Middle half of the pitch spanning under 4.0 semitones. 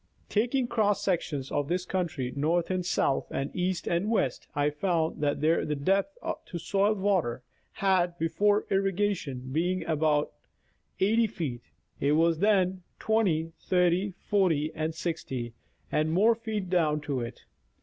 No: average, 4.5 semitones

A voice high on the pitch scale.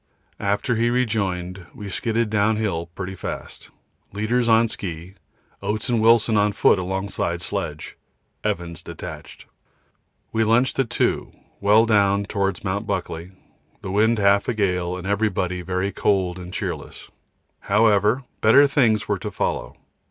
No: low, 100 Hz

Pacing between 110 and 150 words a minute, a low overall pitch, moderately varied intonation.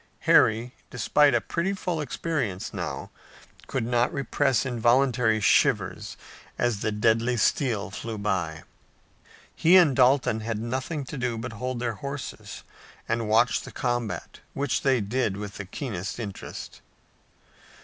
Yes: slow, 135 wpm; low, 120 Hz; average, 3.5 semitones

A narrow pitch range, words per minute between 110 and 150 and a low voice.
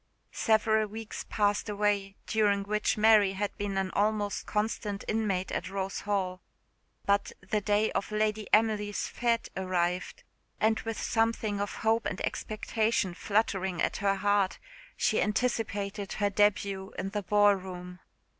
No: narrow, 1.8 semitones; average, 140 wpm; high, 205 Hz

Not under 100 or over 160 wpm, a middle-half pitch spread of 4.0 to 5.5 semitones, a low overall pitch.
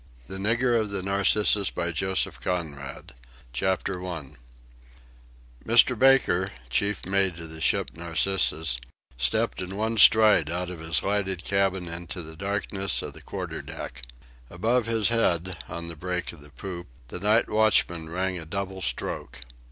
No: average, 145 wpm; average, 3.5 semitones; very low, 95 Hz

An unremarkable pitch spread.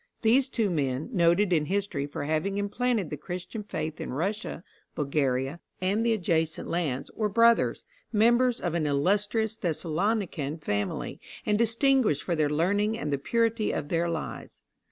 No: wide, 6.1 semitones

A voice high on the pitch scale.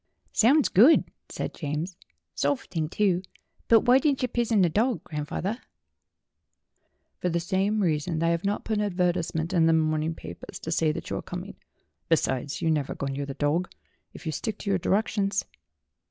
No: medium, 175 Hz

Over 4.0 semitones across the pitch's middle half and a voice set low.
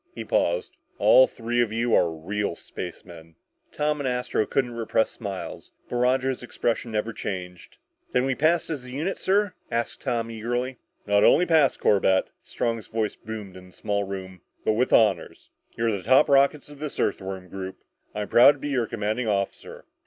Yes: average, 4.7 semitones; low, 115 Hz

